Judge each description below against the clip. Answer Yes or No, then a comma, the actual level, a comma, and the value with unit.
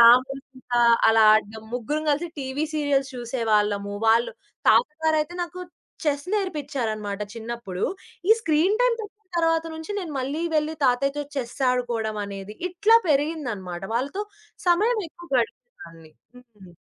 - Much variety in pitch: Yes, wide, 6.2 semitones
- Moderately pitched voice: No, very high, 270 Hz